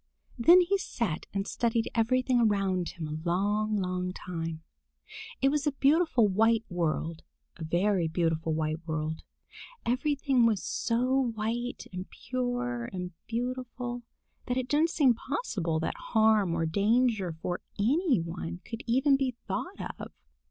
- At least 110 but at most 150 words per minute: Yes, average, 140 wpm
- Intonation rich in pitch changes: Yes, wide, 6.1 semitones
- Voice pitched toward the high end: Yes, high, 220 Hz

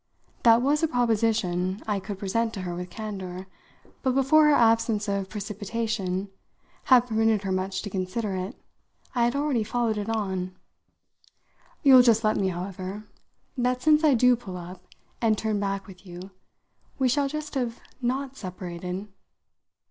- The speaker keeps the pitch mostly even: No, average, 4.3 semitones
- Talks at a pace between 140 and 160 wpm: Yes, average, 155 wpm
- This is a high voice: Yes, high, 215 Hz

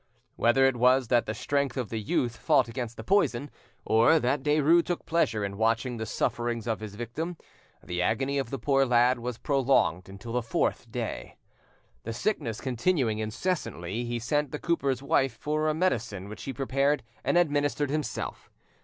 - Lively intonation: No, average, 4.2 semitones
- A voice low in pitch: Yes, low, 125 Hz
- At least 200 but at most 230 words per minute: No, average, 170 wpm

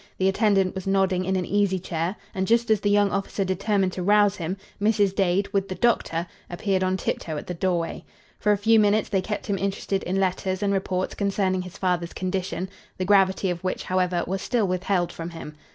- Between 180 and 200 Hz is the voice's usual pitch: Yes, high, 190 Hz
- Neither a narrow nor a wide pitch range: No, narrow, 1.6 semitones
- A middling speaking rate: No, fast, 210 wpm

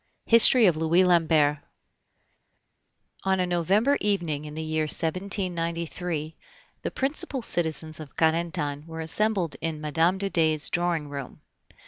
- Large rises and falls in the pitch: No, average, 2.9 semitones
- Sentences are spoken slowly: Yes, slow, 125 wpm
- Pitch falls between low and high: Yes, medium, 165 Hz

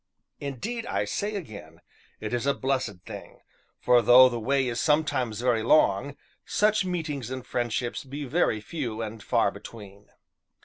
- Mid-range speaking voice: No, low, 130 Hz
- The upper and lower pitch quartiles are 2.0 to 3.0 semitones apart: No, average, 4.5 semitones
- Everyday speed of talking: Yes, average, 150 wpm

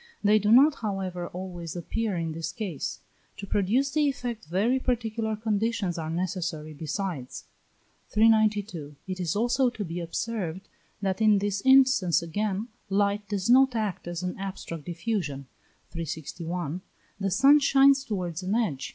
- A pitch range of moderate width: Yes, average, 4.6 semitones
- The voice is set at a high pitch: Yes, high, 195 Hz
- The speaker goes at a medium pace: Yes, average, 145 wpm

